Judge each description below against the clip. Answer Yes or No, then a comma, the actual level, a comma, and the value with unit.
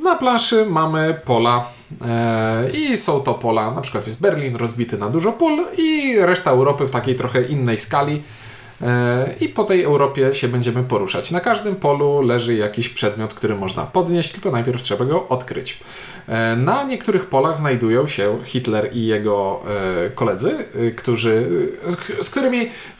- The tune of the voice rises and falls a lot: Yes, wide, 7.7 semitones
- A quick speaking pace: Yes, fast, 165 wpm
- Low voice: Yes, low, 130 Hz